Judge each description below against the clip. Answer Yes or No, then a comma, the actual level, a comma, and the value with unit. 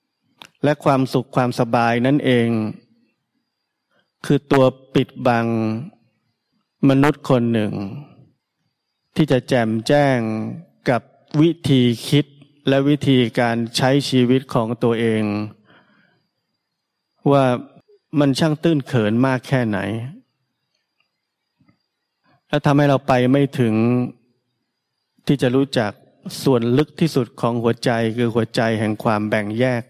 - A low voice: Yes, low, 130 Hz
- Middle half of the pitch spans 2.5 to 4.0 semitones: Yes, average, 3.2 semitones